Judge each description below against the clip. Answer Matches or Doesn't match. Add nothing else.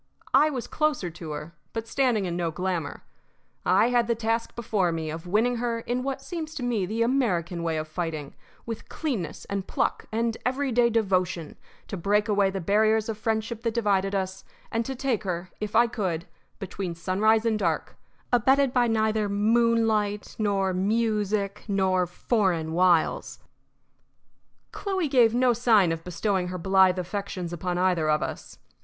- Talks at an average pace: Matches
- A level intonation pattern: Doesn't match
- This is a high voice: Matches